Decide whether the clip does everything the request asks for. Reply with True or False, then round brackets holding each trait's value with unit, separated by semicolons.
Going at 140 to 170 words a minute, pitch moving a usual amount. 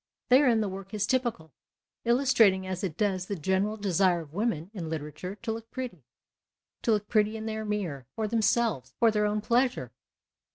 False (180 wpm; 3.5 semitones)